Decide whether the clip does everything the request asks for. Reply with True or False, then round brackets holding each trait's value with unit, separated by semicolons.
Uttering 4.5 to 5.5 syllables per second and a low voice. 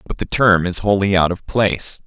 True (5.2 syllables/s; 95 Hz)